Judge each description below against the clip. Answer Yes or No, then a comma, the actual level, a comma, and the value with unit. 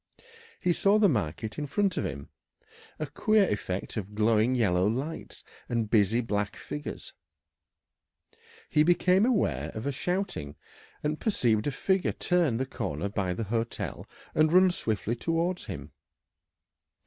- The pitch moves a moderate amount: No, wide, 9.0 semitones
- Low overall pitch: Yes, low, 125 Hz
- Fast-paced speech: No, average, 140 wpm